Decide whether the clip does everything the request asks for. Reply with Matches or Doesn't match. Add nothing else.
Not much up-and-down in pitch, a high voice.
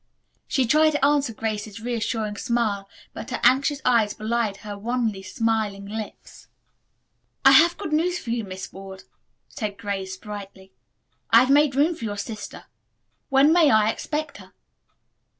Doesn't match